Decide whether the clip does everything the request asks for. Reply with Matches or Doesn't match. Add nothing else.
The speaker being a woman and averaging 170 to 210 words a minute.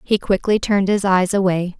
Matches